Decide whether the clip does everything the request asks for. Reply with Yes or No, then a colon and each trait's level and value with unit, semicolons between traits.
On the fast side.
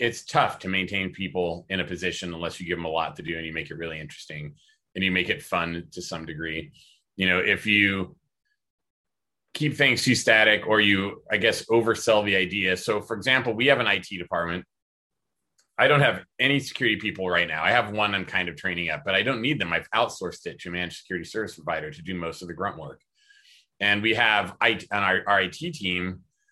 Yes: fast, 215 wpm